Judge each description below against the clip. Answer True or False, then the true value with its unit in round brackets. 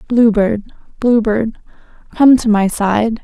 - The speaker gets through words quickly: False (150 wpm)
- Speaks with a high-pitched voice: True (220 Hz)